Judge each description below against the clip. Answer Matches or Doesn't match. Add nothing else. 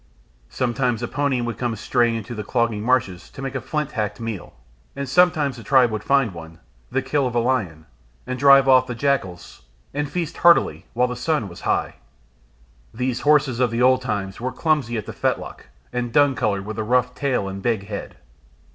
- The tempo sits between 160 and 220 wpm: Matches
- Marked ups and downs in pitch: Doesn't match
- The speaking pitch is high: Doesn't match